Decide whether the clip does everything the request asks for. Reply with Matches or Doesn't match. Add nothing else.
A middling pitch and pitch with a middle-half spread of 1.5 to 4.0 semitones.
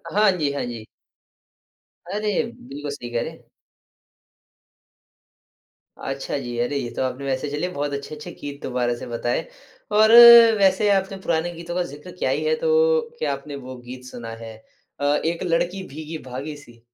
Doesn't match